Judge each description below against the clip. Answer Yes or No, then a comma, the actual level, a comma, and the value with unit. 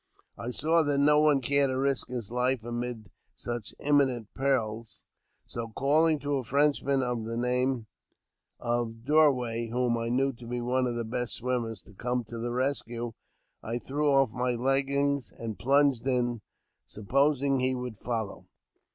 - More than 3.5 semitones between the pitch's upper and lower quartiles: No, average, 2.7 semitones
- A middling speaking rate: Yes, average, 160 wpm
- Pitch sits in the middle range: No, low, 125 Hz